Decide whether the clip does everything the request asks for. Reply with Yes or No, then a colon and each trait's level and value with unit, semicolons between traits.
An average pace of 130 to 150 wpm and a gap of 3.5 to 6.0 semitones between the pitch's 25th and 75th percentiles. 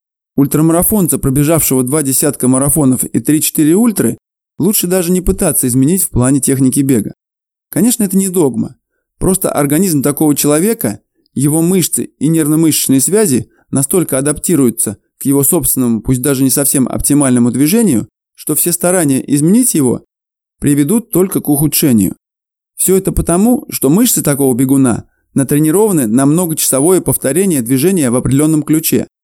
Yes: average, 135 wpm; average, 5.0 semitones